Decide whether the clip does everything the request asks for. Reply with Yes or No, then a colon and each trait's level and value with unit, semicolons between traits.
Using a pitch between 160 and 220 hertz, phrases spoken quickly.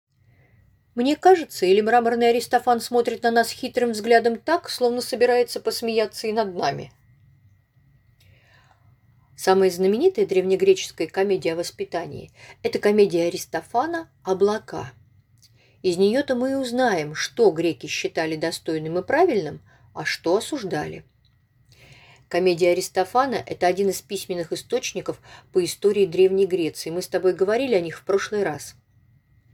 No: high, 190 Hz; average, 125 wpm